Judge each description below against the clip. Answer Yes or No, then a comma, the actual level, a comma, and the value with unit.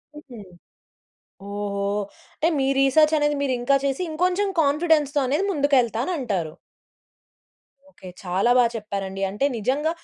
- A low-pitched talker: No, very high, 270 Hz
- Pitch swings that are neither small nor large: No, wide, 6.4 semitones